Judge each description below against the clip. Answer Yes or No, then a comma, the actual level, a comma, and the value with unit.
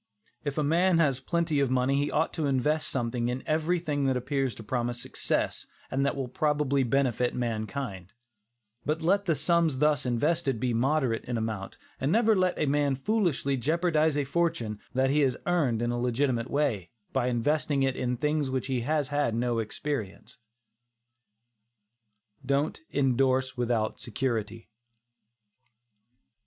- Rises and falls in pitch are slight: No, average, 3.8 semitones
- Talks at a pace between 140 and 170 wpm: Yes, average, 155 wpm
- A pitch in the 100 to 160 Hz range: Yes, low, 135 Hz